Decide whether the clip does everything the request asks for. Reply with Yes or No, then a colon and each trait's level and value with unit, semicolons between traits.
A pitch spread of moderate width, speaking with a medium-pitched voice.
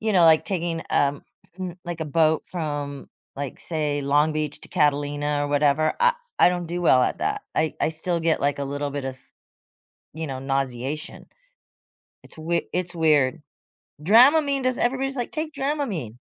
Yes: average, 4.0 semitones; medium, 155 Hz